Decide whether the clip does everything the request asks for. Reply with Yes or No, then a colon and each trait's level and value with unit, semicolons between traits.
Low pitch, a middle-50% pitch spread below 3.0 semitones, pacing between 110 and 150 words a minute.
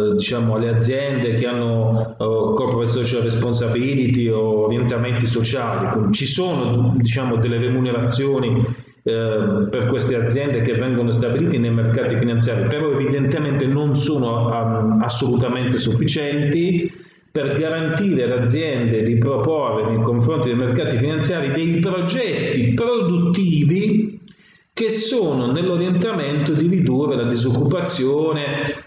No: low, 125 Hz; average, 4.5 semitones; slow, 115 wpm